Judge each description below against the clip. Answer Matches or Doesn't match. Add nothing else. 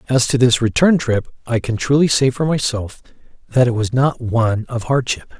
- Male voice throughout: Matches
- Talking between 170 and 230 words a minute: Matches